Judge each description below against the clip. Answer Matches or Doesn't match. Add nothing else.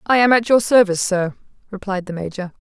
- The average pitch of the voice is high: Matches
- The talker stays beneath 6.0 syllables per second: Doesn't match